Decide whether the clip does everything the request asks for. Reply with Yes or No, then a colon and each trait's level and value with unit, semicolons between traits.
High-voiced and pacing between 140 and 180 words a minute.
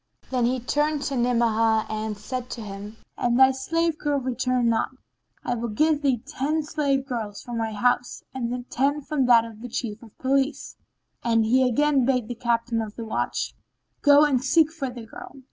No: high, 245 Hz; average, 190 wpm